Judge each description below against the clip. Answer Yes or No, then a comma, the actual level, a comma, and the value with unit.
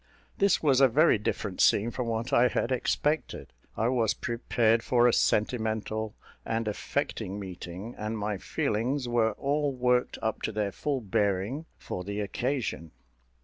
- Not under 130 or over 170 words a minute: Yes, average, 150 wpm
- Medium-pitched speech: No, low, 115 Hz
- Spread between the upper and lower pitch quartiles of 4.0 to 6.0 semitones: No, average, 3.2 semitones